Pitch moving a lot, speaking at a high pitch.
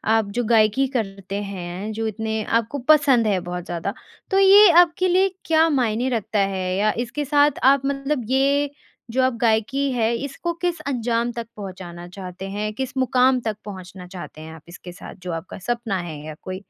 Yes: wide, 5.8 semitones; high, 225 Hz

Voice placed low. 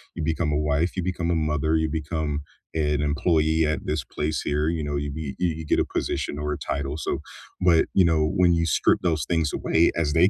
Yes: very low, 80 Hz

